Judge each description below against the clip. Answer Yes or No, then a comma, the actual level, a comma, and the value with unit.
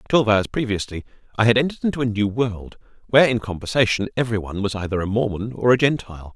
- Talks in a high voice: No, low, 110 Hz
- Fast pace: Yes, fast, 210 wpm